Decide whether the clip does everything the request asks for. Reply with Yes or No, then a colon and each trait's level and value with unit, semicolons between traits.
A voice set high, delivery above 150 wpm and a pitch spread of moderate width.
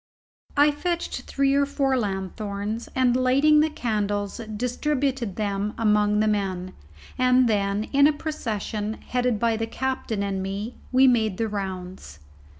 No: high, 220 Hz; average, 145 wpm; average, 4.3 semitones